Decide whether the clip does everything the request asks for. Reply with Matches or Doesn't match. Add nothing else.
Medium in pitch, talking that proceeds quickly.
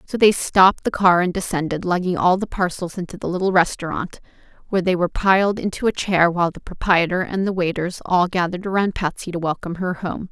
Matches